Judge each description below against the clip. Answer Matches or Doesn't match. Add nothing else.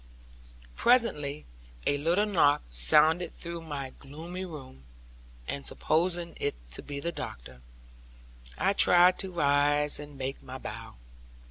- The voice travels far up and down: Doesn't match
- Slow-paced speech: Matches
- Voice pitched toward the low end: Doesn't match